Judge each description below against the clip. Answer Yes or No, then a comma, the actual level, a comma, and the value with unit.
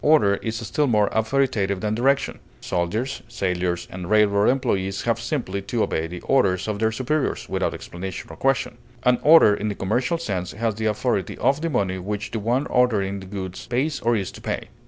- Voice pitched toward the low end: Yes, low, 110 Hz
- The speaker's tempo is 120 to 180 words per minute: No, average, 195 wpm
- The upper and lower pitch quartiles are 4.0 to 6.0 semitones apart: Yes, average, 4.4 semitones